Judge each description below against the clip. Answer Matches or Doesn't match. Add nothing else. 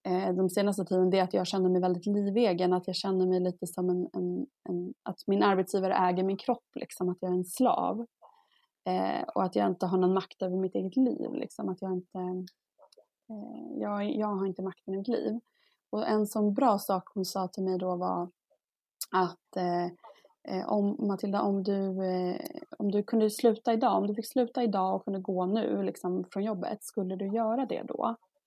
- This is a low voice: Doesn't match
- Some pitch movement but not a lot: Matches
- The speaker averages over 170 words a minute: Matches